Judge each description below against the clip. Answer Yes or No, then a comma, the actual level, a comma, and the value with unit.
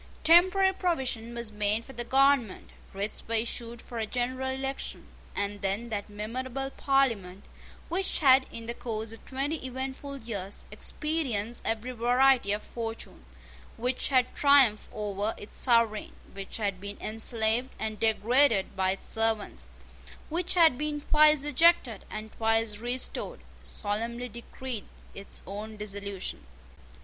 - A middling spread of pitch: Yes, average, 4.0 semitones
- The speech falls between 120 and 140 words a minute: Yes, slow, 135 wpm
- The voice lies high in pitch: Yes, high, 235 Hz